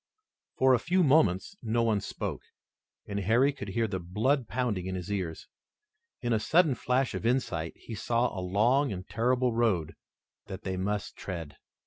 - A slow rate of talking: No, average, 170 wpm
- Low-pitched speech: Yes, low, 110 Hz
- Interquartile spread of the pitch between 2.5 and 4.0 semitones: No, average, 5.0 semitones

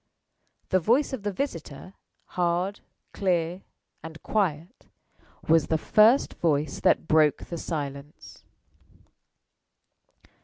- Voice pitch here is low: No, medium, 170 Hz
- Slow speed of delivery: Yes, slow, 100 wpm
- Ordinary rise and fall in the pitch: Yes, average, 4.2 semitones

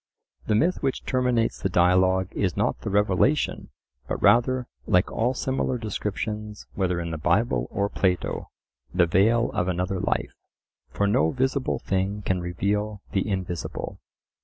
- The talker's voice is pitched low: Yes, low, 100 Hz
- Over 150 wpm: No, average, 145 wpm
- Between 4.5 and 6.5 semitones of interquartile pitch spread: No, average, 4.0 semitones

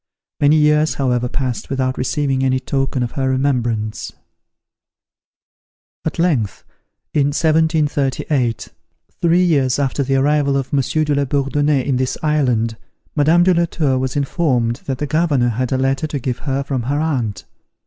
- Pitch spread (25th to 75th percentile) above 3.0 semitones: No, average, 2.7 semitones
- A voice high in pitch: No, low, 135 Hz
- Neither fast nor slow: Yes, average, 155 wpm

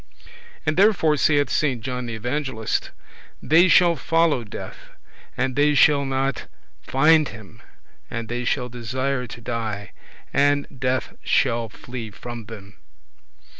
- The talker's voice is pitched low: Yes, low, 130 Hz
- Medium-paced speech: No, slow, 130 wpm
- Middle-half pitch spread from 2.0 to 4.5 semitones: Yes, average, 4.0 semitones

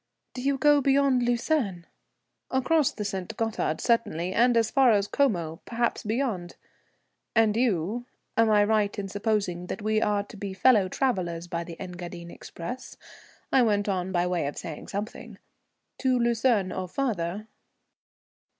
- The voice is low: No, high, 210 Hz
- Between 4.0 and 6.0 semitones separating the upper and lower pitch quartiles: Yes, average, 5.0 semitones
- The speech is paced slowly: No, average, 150 wpm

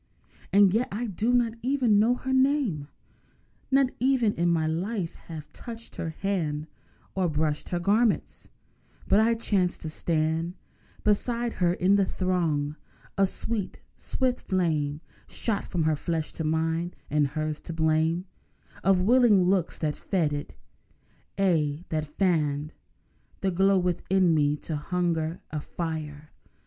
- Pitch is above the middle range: No, medium, 175 Hz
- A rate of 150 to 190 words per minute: No, average, 140 wpm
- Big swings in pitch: No, average, 4.6 semitones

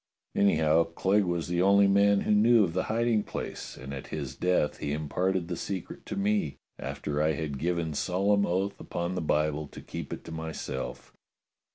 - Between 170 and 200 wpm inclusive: Yes, average, 185 wpm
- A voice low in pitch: Yes, very low, 90 Hz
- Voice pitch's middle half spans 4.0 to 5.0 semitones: Yes, average, 4.4 semitones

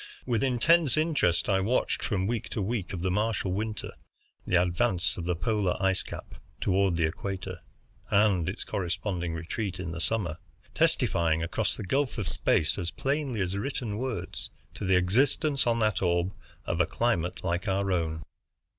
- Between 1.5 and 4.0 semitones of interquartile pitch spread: No, average, 4.4 semitones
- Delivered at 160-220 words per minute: Yes, average, 170 wpm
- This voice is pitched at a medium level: No, very low, 95 Hz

